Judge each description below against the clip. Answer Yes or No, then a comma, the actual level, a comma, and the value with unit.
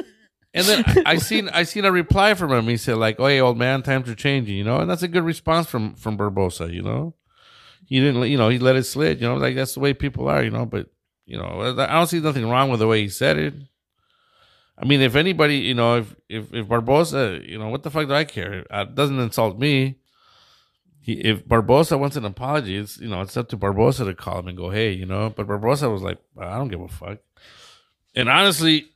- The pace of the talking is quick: Yes, fast, 245 wpm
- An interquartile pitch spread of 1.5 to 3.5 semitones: No, average, 5.1 semitones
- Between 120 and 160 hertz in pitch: Yes, low, 125 Hz